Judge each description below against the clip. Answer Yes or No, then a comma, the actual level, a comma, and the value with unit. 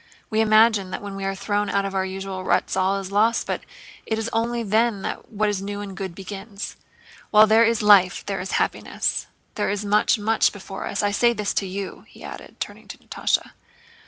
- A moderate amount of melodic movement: No, narrow, 1.9 semitones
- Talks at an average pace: No, fast, 215 wpm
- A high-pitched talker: Yes, high, 205 Hz